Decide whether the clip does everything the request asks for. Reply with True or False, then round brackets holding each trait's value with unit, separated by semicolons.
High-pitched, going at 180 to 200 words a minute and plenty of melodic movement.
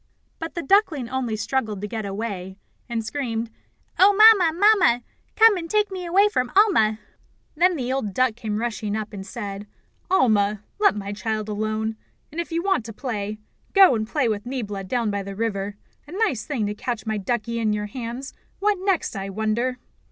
True (230 Hz; 190 wpm; 7.6 semitones)